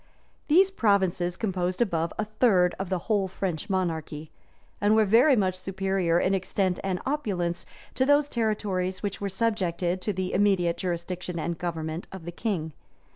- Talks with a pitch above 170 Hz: Yes, medium, 185 Hz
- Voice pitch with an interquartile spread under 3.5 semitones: Yes, average, 3.1 semitones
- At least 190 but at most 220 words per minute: No, average, 155 wpm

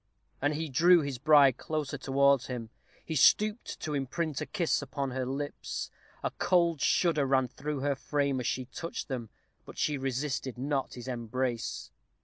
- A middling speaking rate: Yes, average, 165 wpm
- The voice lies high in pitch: No, medium, 140 Hz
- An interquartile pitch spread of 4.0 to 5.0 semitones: No, narrow, 2.6 semitones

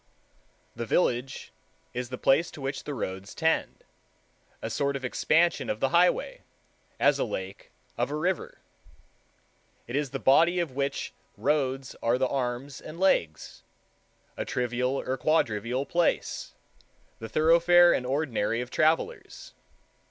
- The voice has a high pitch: No, low, 135 Hz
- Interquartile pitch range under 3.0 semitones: No, average, 4.7 semitones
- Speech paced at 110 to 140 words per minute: Yes, slow, 135 wpm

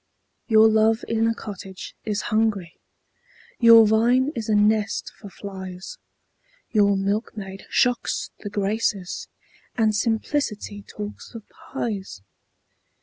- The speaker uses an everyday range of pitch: No, narrow, 2.0 semitones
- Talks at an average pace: No, slow, 110 wpm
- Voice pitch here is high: Yes, high, 215 Hz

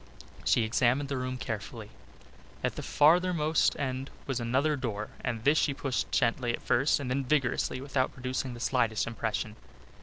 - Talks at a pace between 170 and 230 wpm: No, average, 160 wpm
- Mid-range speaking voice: No, low, 130 Hz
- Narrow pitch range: No, average, 3.0 semitones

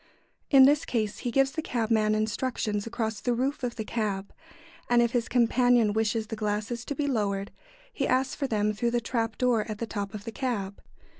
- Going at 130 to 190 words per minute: No, fast, 205 wpm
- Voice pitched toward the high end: Yes, high, 230 Hz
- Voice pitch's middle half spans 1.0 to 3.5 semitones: Yes, average, 2.7 semitones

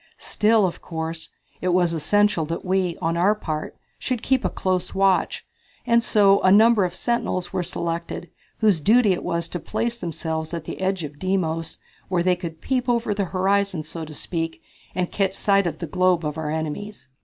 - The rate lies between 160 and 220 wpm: Yes, average, 190 wpm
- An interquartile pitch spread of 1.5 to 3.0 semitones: No, average, 3.6 semitones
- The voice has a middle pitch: Yes, medium, 180 Hz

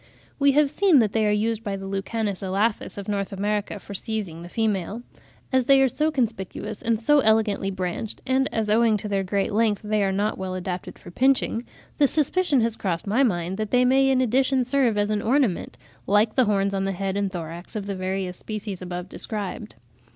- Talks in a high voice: Yes, high, 210 Hz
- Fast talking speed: Yes, fast, 210 wpm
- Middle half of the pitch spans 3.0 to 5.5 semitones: Yes, average, 3.5 semitones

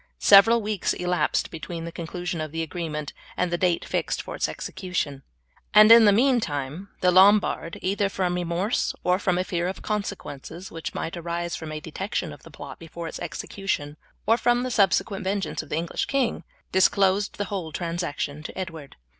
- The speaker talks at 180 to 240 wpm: Yes, average, 185 wpm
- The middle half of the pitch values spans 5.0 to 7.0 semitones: No, average, 3.4 semitones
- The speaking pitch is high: No, medium, 180 Hz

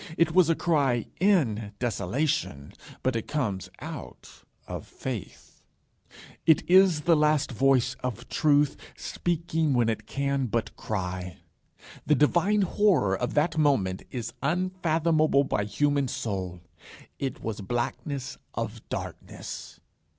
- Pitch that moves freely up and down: Yes, wide, 5.8 semitones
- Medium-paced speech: No, slow, 120 wpm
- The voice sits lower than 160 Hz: Yes, medium, 140 Hz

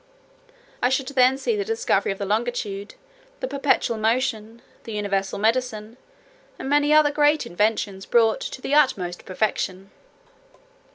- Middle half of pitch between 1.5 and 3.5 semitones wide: No, average, 4.9 semitones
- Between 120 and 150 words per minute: Yes, slow, 135 wpm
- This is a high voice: Yes, high, 230 Hz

